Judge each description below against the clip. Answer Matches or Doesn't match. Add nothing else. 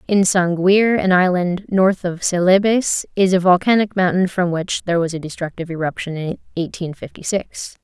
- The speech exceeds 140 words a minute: Matches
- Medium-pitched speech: Matches